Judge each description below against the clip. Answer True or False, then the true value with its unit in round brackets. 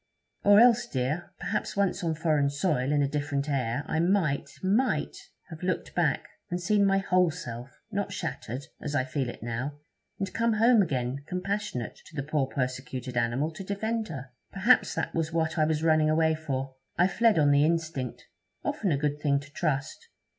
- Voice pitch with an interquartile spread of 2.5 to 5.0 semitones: False (5.4 semitones)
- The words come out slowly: False (190 wpm)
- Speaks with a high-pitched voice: False (155 Hz)